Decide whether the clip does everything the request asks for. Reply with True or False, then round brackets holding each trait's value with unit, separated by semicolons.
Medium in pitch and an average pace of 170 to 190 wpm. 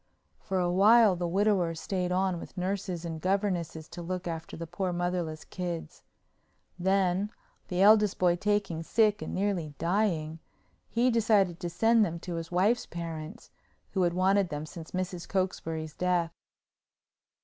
False (180 Hz; 150 wpm)